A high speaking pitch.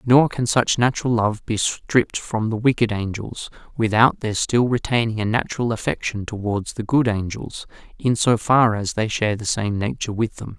No: low, 115 Hz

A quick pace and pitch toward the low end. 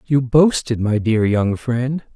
No: average, 165 wpm; low, 125 Hz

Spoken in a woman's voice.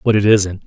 No: male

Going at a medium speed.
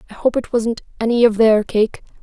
No: fast, 215 wpm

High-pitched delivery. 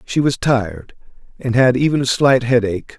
No: low, 125 Hz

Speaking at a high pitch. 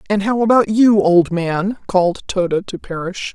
Yes: high, 195 Hz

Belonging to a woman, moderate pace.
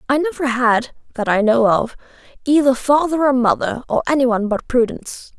Yes: female; average, 180 wpm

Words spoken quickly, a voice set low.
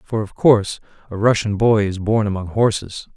No: average, 190 wpm; low, 105 Hz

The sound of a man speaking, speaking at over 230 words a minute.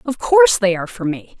No: female; fast, 255 wpm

